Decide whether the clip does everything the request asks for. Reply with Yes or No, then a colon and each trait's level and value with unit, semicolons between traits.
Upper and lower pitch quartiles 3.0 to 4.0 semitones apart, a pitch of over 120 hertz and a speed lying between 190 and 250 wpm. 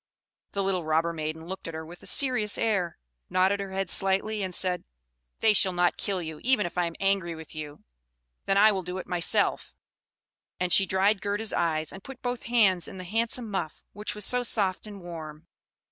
Yes: average, 3.3 semitones; high, 190 Hz; fast, 205 wpm